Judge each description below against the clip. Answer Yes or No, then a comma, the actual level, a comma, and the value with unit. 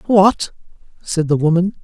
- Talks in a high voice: No, medium, 175 Hz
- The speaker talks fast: No, slow, 130 wpm